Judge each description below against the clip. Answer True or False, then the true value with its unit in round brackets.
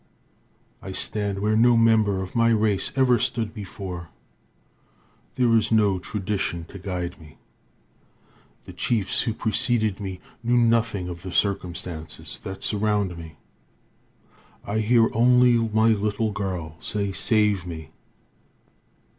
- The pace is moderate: False (125 wpm)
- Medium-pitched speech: False (105 Hz)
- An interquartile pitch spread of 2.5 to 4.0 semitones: True (3.4 semitones)